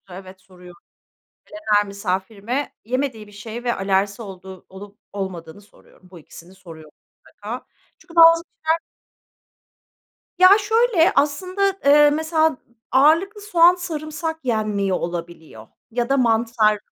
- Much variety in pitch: Yes, wide, 8.6 semitones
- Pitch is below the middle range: No, high, 225 Hz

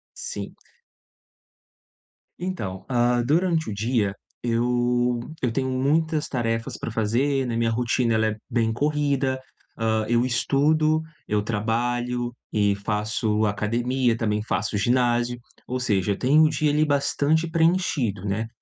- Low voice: Yes, low, 120 Hz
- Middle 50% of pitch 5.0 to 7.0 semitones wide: No, average, 3.8 semitones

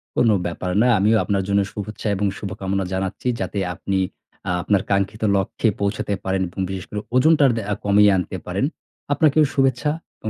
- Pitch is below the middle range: Yes, low, 100 Hz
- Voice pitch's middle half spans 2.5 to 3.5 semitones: Yes, average, 2.8 semitones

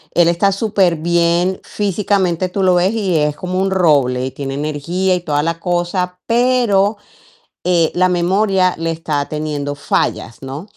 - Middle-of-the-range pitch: Yes, medium, 175 Hz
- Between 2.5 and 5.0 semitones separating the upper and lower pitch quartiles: Yes, average, 3.7 semitones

